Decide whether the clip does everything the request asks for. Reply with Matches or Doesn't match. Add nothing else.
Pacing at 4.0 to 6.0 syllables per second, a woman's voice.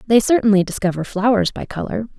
Doesn't match